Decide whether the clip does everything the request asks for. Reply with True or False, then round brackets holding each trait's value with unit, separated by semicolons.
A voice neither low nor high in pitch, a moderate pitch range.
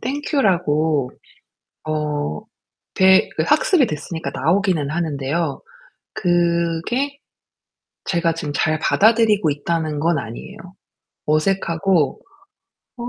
True (170 Hz; 4.3 semitones)